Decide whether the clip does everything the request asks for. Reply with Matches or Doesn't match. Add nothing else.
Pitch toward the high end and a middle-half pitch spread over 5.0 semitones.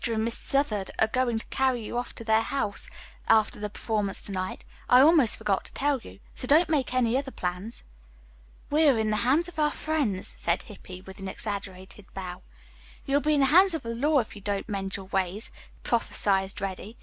Matches